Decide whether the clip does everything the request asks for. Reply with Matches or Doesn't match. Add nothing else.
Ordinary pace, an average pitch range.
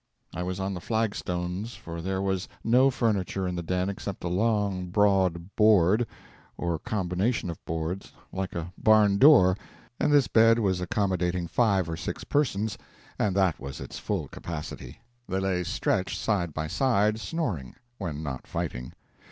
Matches